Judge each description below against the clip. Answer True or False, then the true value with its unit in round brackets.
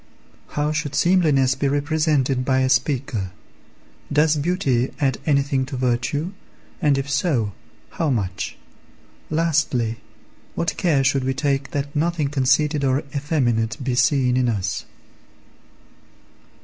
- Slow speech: True (125 wpm)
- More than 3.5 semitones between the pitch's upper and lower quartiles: False (2.7 semitones)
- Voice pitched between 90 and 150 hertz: True (140 Hz)